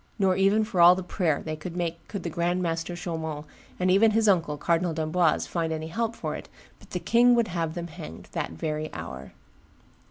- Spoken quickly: Yes, fast, 210 wpm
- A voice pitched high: No, medium, 170 Hz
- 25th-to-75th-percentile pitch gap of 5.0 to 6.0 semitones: No, average, 3.0 semitones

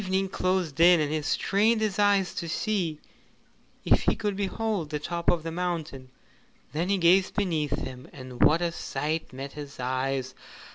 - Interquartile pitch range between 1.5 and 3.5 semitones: No, average, 4.6 semitones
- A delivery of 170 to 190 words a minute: Yes, average, 175 wpm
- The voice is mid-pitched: Yes, medium, 170 Hz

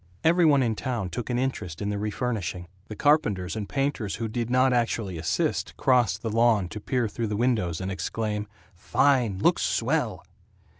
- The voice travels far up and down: No, average, 3.8 semitones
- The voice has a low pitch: Yes, low, 110 Hz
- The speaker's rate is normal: Yes, average, 180 wpm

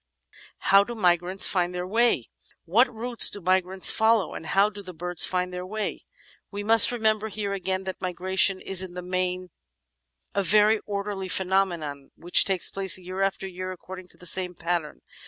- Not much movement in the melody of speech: Yes, narrow, 2.1 semitones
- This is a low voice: No, high, 190 Hz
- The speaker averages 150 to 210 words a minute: Yes, average, 175 wpm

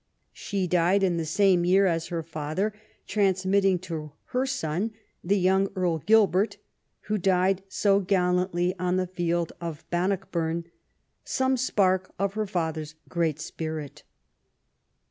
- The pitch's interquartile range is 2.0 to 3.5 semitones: Yes, average, 2.7 semitones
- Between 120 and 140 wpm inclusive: Yes, slow, 135 wpm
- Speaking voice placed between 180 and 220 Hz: Yes, medium, 185 Hz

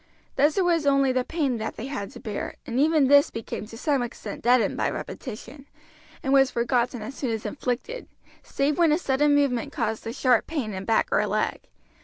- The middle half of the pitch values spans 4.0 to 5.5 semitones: No, average, 3.6 semitones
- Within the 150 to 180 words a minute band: No, fast, 205 wpm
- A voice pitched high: Yes, very high, 265 Hz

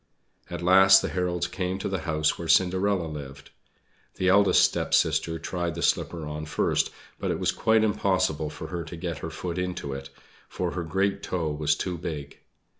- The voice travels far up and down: No, average, 3.2 semitones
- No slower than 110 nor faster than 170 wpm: No, average, 185 wpm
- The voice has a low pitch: Yes, very low, 85 Hz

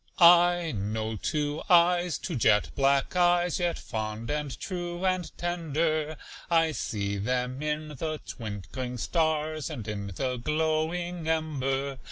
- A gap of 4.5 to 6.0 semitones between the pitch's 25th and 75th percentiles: Yes, average, 5.2 semitones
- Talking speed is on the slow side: Yes, slow, 130 wpm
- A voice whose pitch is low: No, medium, 150 Hz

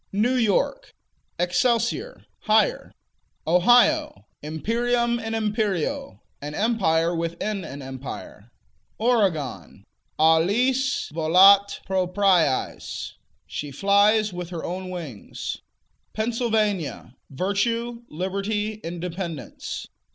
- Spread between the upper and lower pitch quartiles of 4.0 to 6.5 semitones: Yes, wide, 5.5 semitones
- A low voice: No, high, 195 Hz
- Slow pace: Yes, slow, 80 wpm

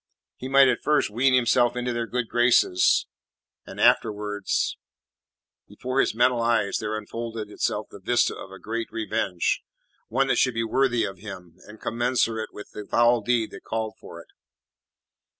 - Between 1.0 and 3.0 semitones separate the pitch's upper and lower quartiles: Yes, narrow, 2.6 semitones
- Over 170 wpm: No, average, 165 wpm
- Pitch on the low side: Yes, low, 115 Hz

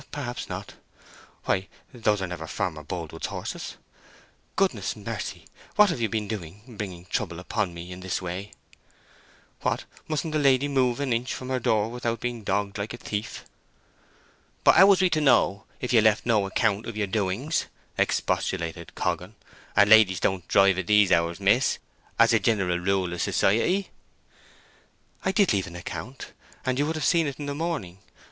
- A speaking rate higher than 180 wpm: No, average, 170 wpm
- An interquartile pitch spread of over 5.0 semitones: Yes, wide, 5.6 semitones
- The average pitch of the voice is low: Yes, low, 105 Hz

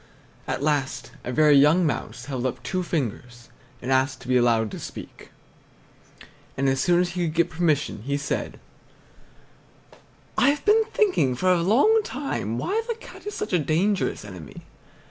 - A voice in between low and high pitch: Yes, medium, 150 Hz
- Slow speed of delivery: No, average, 165 wpm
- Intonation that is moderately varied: No, wide, 6.5 semitones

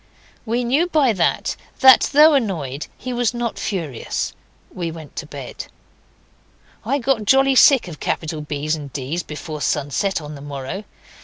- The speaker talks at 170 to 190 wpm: No, average, 155 wpm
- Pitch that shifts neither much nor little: No, wide, 8.7 semitones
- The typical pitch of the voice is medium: Yes, medium, 175 Hz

